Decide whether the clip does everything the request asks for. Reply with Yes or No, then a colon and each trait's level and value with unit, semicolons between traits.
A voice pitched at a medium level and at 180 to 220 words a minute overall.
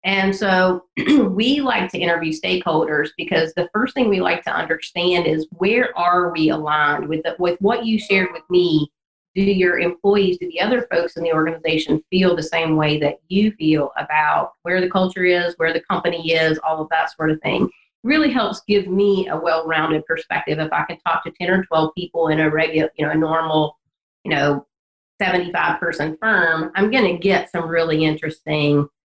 Yes: medium, 170 Hz; average, 195 wpm